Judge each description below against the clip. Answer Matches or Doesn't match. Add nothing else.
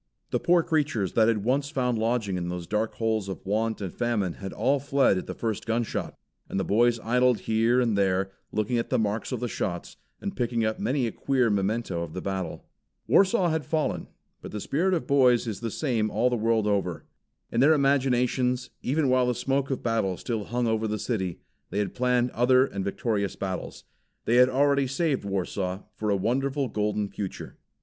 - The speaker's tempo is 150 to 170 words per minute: Doesn't match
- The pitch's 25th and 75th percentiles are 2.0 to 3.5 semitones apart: Doesn't match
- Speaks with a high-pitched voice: Doesn't match